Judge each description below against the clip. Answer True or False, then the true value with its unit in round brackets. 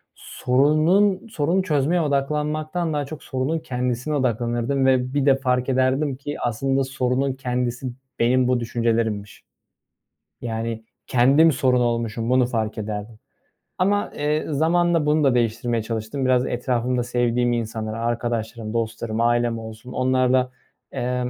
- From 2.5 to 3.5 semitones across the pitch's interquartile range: True (3.2 semitones)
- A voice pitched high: False (125 Hz)